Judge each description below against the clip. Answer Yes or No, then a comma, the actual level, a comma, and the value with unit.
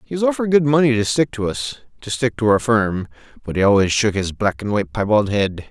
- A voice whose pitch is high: No, low, 110 Hz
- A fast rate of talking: Yes, fast, 230 wpm